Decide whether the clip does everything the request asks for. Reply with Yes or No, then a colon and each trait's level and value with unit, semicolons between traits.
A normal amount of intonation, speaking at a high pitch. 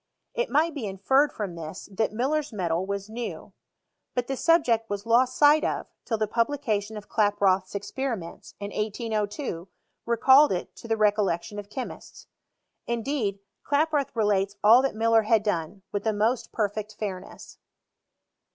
Yes: average, 4.0 semitones; high, 215 Hz